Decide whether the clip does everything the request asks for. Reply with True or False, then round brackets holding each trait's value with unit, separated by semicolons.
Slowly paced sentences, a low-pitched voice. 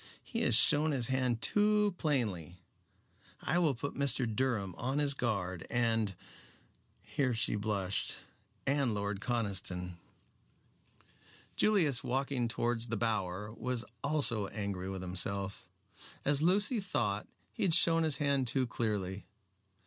True (125 wpm; 120 Hz)